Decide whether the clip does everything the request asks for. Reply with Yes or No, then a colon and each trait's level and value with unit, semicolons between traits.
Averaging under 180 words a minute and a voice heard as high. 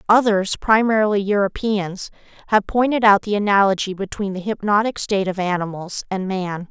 Yes: average, 145 wpm; high, 200 Hz